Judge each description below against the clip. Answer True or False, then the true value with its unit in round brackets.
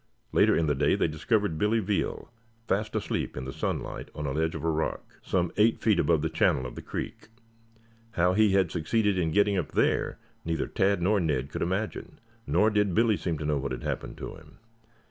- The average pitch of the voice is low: True (85 Hz)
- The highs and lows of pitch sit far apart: False (5.0 semitones)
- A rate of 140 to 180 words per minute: False (205 wpm)